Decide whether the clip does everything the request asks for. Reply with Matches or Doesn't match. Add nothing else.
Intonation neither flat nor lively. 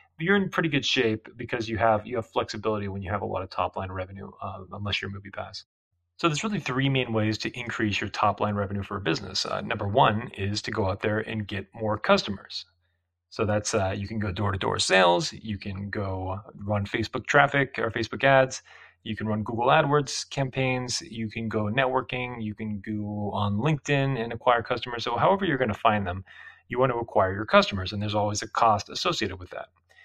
Matches